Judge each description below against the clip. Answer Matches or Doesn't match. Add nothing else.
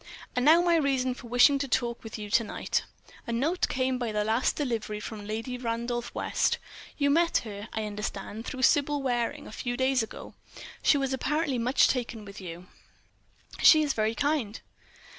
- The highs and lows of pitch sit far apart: Doesn't match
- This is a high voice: Matches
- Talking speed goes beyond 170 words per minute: Matches